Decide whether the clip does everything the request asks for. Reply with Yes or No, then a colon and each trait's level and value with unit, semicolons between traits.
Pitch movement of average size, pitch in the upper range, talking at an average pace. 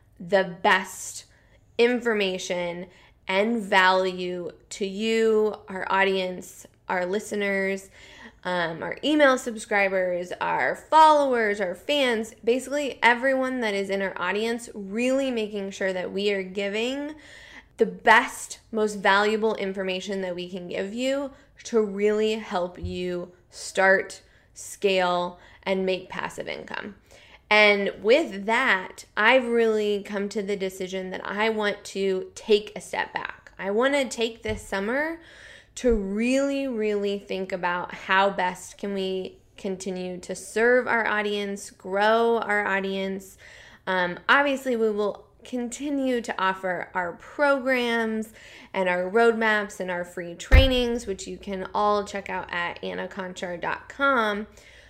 No: average, 3.5 semitones; high, 205 Hz; slow, 130 wpm